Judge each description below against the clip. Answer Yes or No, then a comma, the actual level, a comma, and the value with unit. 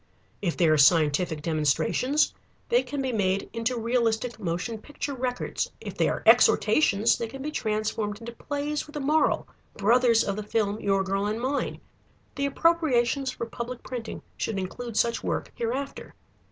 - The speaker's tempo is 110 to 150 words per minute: No, average, 165 wpm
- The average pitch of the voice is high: Yes, high, 230 Hz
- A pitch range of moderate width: Yes, average, 4.7 semitones